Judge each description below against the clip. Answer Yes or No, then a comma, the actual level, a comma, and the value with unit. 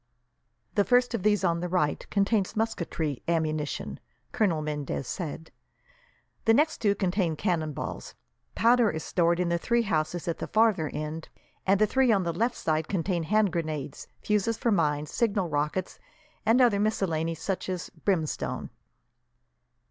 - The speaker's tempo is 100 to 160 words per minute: Yes, average, 150 wpm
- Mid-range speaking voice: Yes, medium, 180 Hz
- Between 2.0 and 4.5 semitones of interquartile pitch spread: No, average, 5.1 semitones